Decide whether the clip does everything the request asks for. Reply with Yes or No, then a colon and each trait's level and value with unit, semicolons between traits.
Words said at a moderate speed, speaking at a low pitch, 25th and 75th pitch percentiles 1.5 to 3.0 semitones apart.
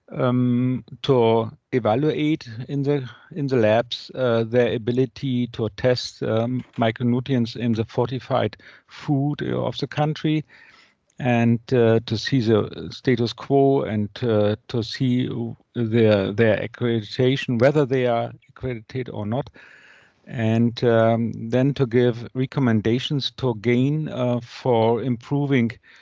No: slow, 120 wpm; low, 125 Hz; narrow, 2.4 semitones